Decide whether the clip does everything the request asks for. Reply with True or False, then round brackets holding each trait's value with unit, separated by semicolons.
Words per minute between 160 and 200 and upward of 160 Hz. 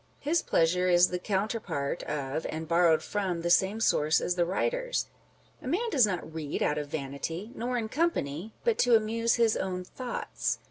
True (180 wpm; 185 Hz)